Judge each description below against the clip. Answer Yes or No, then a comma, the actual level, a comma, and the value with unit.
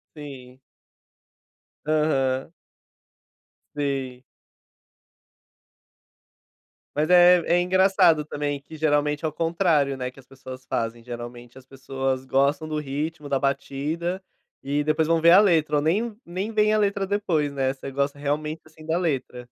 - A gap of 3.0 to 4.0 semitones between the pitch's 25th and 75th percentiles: Yes, average, 3.7 semitones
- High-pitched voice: No, medium, 150 Hz